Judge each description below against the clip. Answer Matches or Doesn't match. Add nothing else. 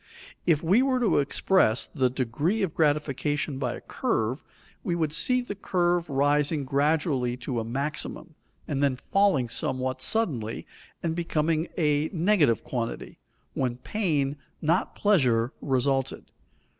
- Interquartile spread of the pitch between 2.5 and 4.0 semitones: Doesn't match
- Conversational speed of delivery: Doesn't match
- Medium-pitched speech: Matches